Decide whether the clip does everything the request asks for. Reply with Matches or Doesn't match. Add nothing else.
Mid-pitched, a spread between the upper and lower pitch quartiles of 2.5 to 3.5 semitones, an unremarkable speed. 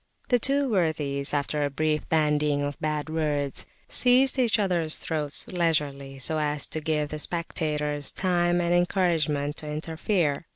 Matches